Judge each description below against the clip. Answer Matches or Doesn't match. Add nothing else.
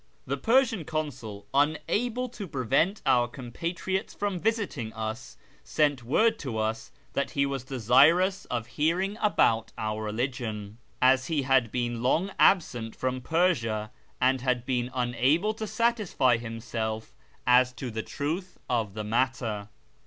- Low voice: Matches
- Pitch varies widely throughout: Matches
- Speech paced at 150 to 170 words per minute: Doesn't match